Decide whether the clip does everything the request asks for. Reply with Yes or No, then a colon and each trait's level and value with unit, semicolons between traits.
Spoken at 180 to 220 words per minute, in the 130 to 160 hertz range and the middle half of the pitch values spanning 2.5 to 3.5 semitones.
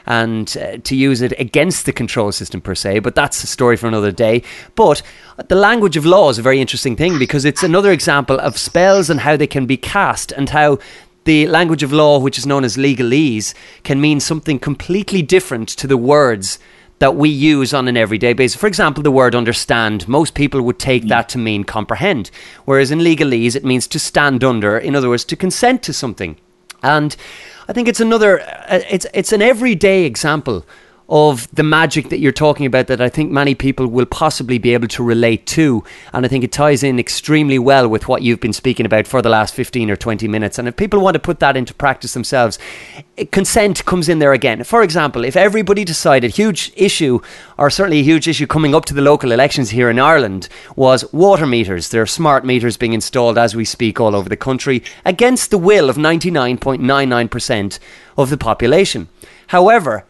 No: fast, 205 wpm; low, 135 Hz; average, 4.6 semitones